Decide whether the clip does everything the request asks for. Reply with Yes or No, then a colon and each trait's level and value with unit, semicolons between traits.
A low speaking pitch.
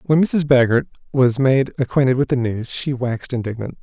Yes: low, 130 Hz